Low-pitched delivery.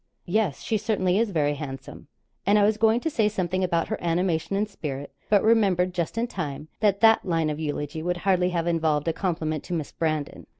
No: medium, 175 Hz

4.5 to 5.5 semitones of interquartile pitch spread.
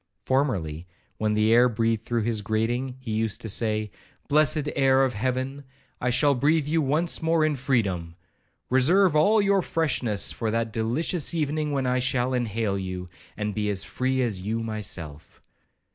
Yes: average, 4.8 semitones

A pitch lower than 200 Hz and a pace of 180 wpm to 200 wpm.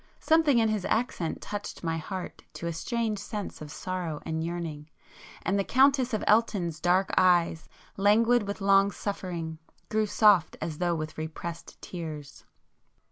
No: medium, 185 Hz; average, 150 wpm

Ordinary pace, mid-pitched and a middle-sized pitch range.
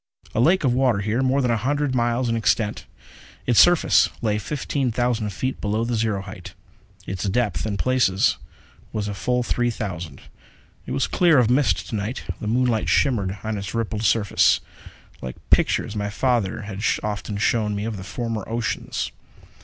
No: average, 175 wpm; low, 110 Hz; average, 3.3 semitones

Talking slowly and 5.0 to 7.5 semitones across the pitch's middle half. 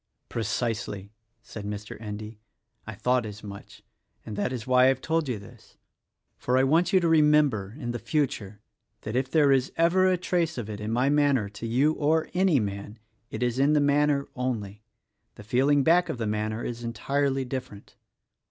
No: average, 195 wpm; average, 5.3 semitones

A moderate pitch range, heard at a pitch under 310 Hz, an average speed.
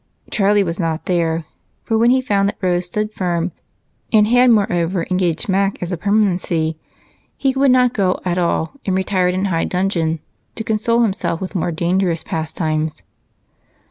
Yes: average, 3.7 semitones; medium, 185 Hz; average, 165 wpm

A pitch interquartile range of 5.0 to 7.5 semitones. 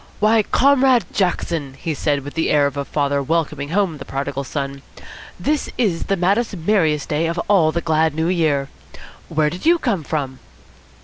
Yes: wide, 5.4 semitones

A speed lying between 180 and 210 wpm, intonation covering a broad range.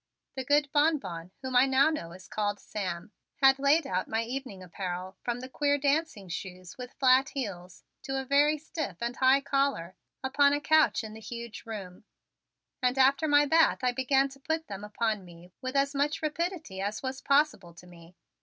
Yes: average, 190 wpm; wide, 6.3 semitones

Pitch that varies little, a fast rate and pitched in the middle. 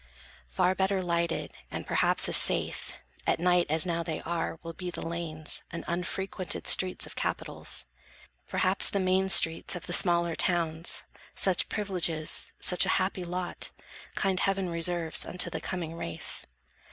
No: narrow, 1.9 semitones; average, 150 wpm; medium, 175 Hz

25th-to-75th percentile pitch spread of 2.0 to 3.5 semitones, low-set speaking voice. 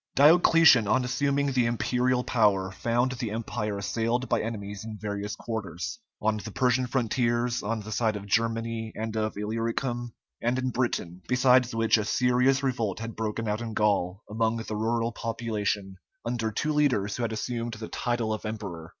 Yes: narrow, 2.5 semitones; low, 115 Hz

